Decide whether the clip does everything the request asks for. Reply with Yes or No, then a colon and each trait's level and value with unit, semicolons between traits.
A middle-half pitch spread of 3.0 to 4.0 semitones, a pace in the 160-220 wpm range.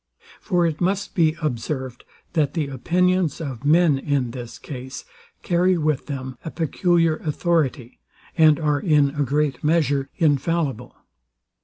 No: average, 3.7 semitones; slow, 135 wpm